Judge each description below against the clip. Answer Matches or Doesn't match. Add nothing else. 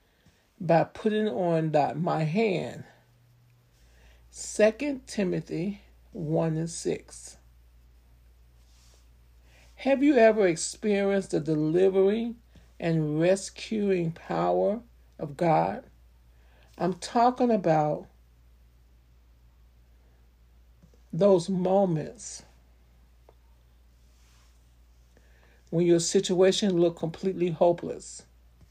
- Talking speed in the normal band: Doesn't match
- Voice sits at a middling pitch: Doesn't match